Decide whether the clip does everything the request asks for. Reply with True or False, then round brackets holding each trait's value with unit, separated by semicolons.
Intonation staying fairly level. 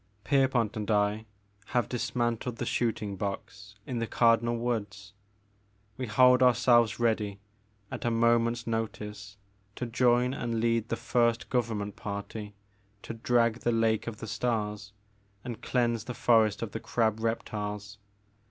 True (2.2 semitones)